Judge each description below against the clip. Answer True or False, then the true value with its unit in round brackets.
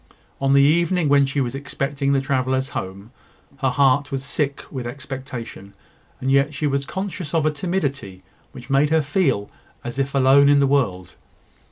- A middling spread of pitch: False (1.7 semitones)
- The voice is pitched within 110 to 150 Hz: True (140 Hz)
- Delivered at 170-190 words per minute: True (175 wpm)